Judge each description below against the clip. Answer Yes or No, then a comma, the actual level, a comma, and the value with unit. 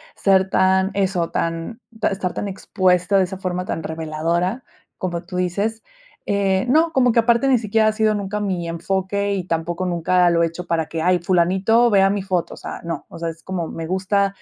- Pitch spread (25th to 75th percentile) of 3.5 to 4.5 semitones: No, average, 2.8 semitones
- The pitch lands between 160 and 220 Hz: Yes, medium, 185 Hz